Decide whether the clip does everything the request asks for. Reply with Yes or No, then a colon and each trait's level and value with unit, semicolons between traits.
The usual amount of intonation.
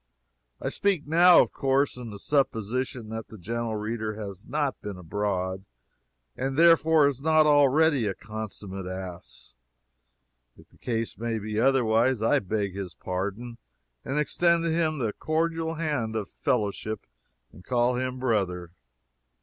No: wide, 5.8 semitones